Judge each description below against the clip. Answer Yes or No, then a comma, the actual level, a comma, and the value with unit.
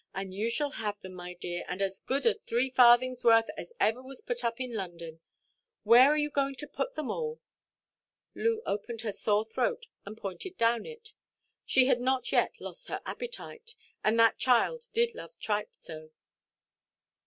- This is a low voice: No, high, 240 Hz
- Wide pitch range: Yes, wide, 6.2 semitones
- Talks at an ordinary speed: Yes, average, 180 wpm